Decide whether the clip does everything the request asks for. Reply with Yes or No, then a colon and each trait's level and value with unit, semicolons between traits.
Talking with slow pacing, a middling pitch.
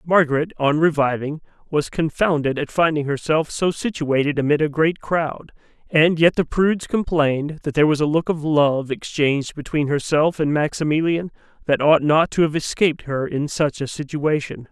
No: average, 170 wpm; medium, 155 Hz